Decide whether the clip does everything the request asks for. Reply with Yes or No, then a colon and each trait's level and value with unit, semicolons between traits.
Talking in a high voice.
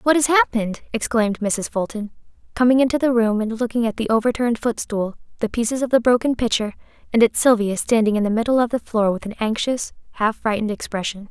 Yes: high, 230 Hz